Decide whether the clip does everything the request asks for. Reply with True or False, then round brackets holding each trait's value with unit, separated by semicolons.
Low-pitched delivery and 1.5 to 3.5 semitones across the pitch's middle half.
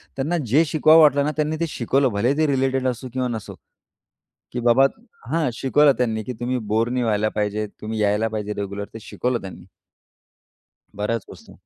False (125 Hz; 4.4 semitones)